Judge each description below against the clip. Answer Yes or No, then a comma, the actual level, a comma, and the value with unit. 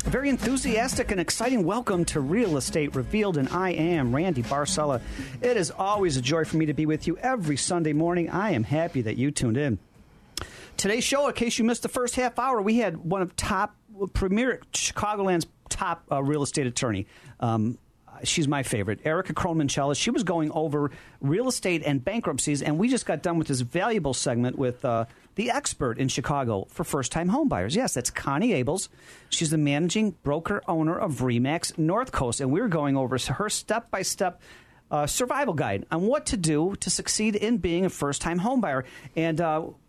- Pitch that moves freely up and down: Yes, wide, 6.2 semitones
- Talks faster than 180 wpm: Yes, average, 195 wpm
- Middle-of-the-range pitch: Yes, medium, 160 Hz